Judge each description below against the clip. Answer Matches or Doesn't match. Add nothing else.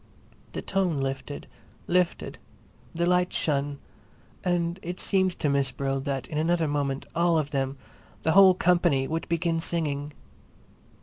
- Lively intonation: Doesn't match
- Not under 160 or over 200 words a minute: Doesn't match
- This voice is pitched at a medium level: Matches